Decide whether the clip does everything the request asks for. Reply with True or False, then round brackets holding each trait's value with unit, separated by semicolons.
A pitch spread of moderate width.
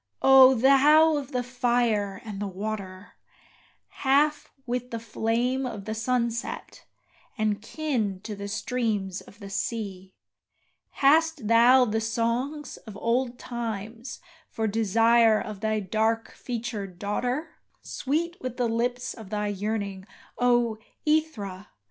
True (3.2 semitones)